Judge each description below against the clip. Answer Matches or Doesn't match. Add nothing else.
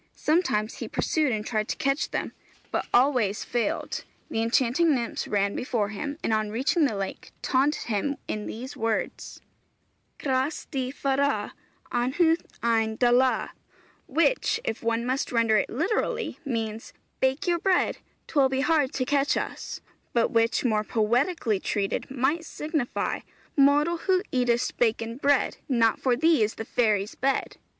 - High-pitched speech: Matches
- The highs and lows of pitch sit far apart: Doesn't match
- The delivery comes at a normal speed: Matches